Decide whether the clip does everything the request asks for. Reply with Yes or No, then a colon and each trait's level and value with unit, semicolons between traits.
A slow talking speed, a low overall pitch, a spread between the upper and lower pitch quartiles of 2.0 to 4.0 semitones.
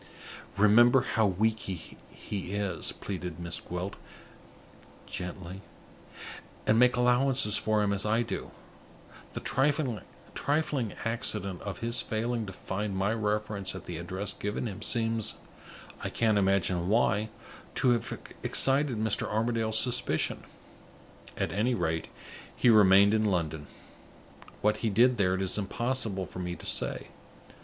Yes: slow, 130 wpm; low, 105 Hz; average, 3.4 semitones